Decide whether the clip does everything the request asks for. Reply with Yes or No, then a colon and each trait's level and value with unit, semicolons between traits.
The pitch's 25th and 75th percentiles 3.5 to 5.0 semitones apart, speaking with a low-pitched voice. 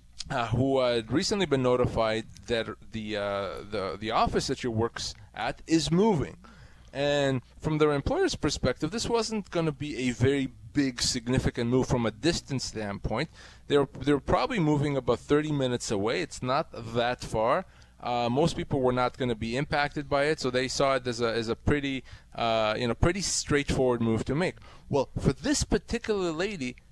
Yes: average, 3.9 semitones; low, 130 Hz